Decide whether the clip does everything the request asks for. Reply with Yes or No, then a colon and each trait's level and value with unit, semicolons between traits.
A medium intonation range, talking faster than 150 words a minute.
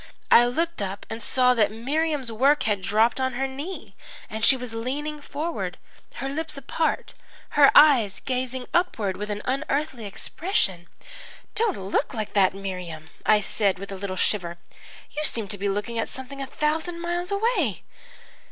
No: wide, 6.5 semitones; average, 165 wpm